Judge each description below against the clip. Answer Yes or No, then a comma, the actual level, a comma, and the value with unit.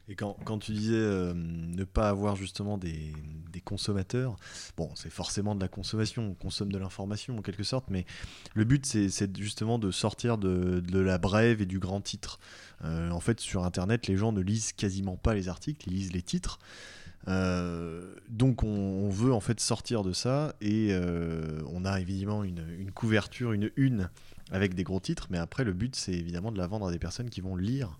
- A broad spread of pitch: No, average, 3.2 semitones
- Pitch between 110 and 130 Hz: No, low, 100 Hz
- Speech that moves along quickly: No, average, 210 wpm